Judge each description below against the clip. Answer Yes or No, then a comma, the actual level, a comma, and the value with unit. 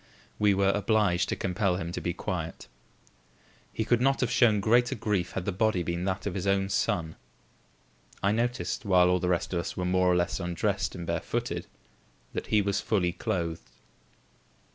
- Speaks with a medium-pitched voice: No, very low, 95 Hz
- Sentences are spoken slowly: No, average, 185 wpm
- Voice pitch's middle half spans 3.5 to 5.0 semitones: No, average, 3.0 semitones